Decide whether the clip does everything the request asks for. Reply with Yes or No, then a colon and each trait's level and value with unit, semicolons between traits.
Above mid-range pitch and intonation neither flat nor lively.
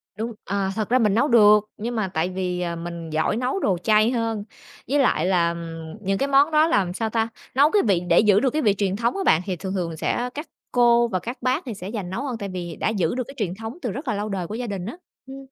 Yes: high, 210 Hz; average, 4.8 semitones